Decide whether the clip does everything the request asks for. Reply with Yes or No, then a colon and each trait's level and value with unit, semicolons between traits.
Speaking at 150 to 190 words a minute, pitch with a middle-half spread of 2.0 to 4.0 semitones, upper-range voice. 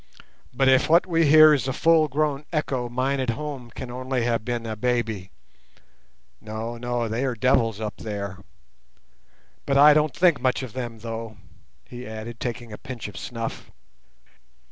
No: average, 165 wpm; average, 3.3 semitones; low, 125 Hz